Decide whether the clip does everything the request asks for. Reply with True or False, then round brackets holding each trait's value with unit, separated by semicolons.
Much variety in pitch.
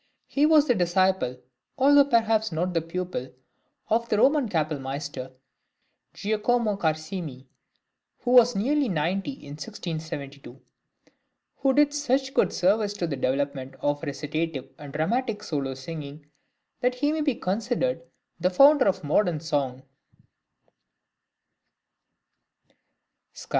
True (8.6 semitones)